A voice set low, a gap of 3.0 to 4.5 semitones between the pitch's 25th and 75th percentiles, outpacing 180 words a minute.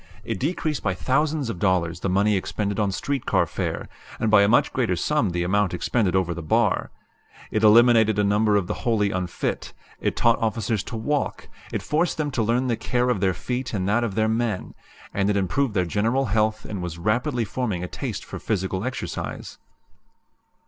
Yes: low, 110 Hz; average, 4.1 semitones; average, 195 wpm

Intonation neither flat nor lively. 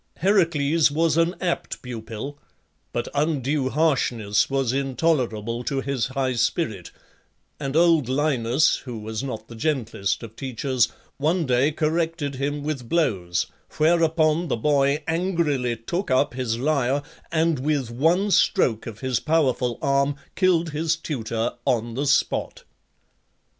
Yes: average, 4.8 semitones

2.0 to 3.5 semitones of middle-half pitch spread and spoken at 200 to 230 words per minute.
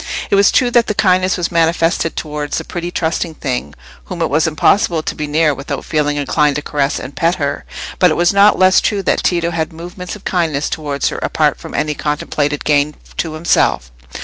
Yes: average, 3.2 semitones; fast, 205 wpm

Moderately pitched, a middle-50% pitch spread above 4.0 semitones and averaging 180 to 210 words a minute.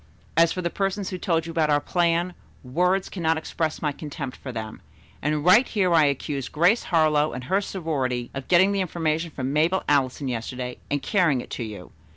Yes: medium, 160 Hz; average, 4.6 semitones; average, 195 wpm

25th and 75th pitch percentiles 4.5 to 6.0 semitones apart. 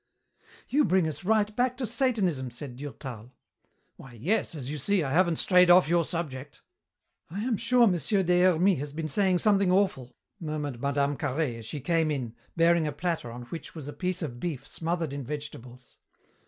Yes: average, 5.1 semitones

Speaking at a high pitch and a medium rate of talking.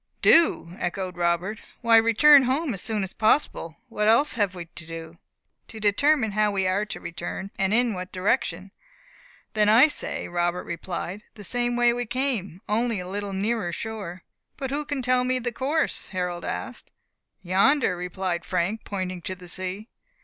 Yes: high, 205 Hz; average, 175 wpm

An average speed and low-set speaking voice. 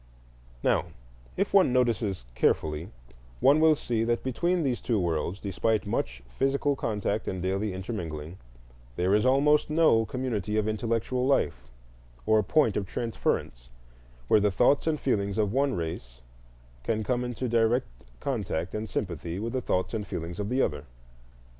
Yes: average, 155 wpm; low, 110 Hz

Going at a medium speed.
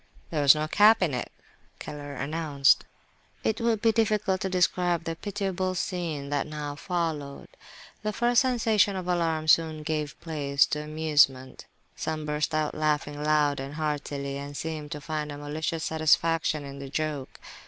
Yes: average, 160 wpm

